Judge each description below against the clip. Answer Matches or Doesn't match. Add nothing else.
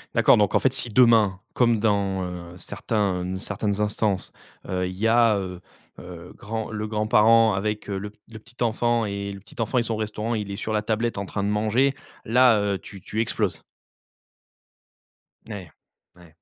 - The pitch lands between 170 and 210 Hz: Doesn't match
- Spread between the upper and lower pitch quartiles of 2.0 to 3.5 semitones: Matches